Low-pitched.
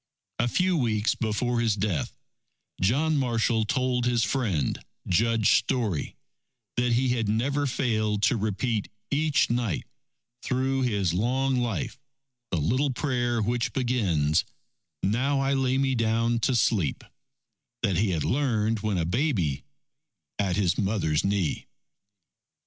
Yes: low, 115 Hz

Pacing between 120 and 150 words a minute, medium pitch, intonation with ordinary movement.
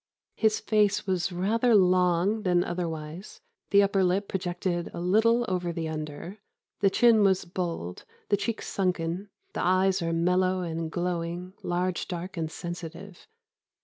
No: average, 145 wpm; medium, 180 Hz; narrow, 2.3 semitones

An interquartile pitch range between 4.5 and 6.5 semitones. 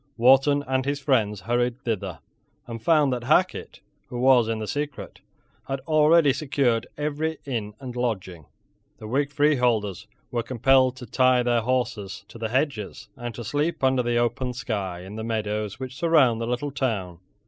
No: average, 3.5 semitones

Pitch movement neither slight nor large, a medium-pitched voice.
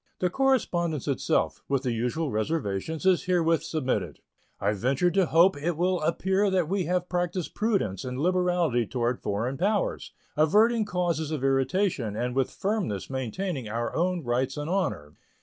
No: wide, 6.2 semitones; medium, 160 Hz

